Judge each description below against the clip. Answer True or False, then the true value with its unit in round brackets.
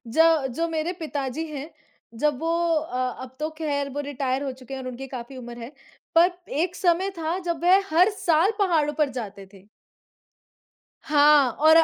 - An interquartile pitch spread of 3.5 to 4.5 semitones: True (4.1 semitones)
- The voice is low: False (300 Hz)